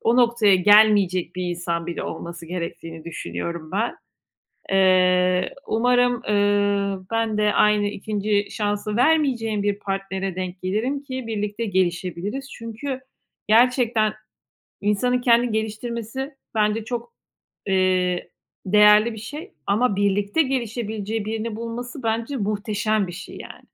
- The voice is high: Yes, high, 210 Hz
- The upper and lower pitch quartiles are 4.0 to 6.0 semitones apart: No, average, 3.3 semitones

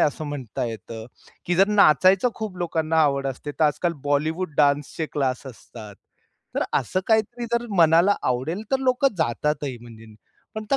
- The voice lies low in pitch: No, medium, 155 Hz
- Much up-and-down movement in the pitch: Yes, wide, 6.1 semitones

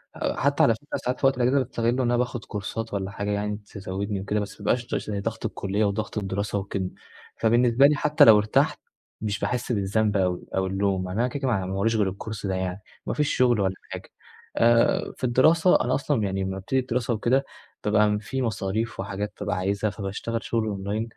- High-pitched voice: No, low, 105 Hz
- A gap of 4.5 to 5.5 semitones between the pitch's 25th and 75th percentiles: No, average, 3.4 semitones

